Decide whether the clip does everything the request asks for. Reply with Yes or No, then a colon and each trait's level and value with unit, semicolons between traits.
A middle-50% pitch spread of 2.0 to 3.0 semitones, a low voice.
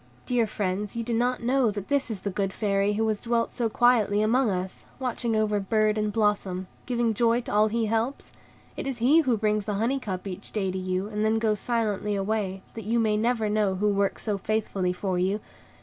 No: narrow, 2.6 semitones; high, 215 Hz